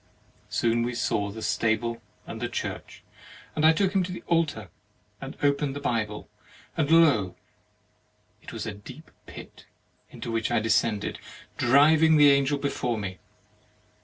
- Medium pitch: No, low, 125 Hz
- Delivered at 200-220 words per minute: No, average, 150 wpm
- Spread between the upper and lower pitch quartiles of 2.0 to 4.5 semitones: No, average, 5.3 semitones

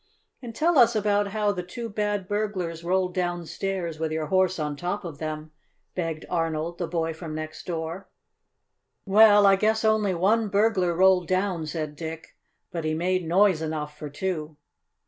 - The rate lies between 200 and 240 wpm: No, average, 165 wpm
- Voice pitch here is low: No, medium, 180 Hz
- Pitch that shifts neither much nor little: Yes, average, 4.0 semitones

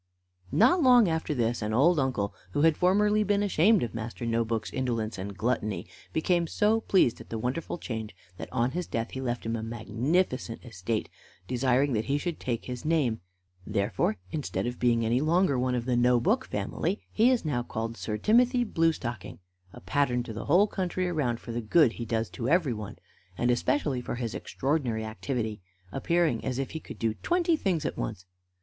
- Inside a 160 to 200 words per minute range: Yes, average, 195 wpm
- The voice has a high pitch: No, low, 125 Hz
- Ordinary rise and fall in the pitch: No, wide, 6.6 semitones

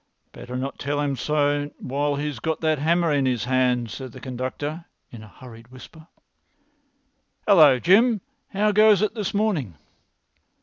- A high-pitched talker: No, medium, 145 Hz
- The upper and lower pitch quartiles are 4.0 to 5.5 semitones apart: Yes, average, 4.9 semitones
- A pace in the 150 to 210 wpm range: Yes, average, 160 wpm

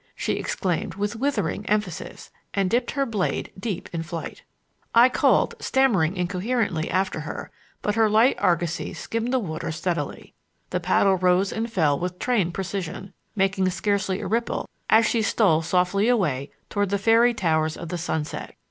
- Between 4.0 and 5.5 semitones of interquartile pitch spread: Yes, average, 4.4 semitones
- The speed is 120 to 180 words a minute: Yes, average, 160 wpm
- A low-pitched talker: No, high, 195 Hz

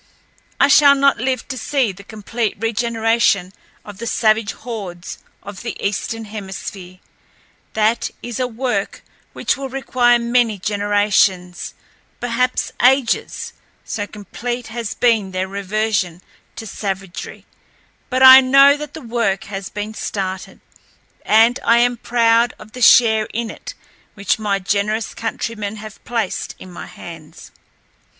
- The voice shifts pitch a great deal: No, average, 3.2 semitones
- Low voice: No, high, 220 Hz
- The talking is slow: Yes, slow, 130 wpm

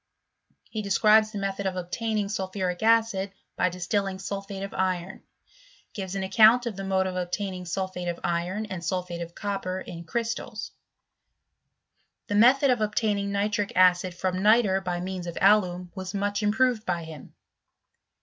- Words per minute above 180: No, average, 160 wpm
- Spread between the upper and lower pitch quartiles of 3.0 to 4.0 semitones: No, narrow, 2.4 semitones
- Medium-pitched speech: No, high, 195 Hz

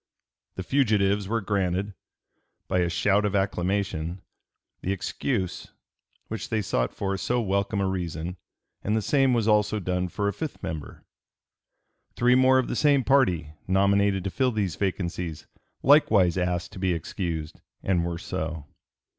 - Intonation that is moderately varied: Yes, average, 3.3 semitones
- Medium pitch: No, very low, 95 Hz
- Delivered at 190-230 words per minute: No, average, 150 wpm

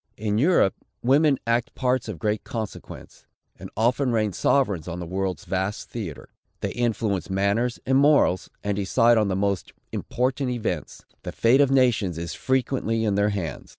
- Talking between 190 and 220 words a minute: No, average, 165 wpm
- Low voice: Yes, low, 110 Hz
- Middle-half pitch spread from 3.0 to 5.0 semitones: Yes, average, 4.4 semitones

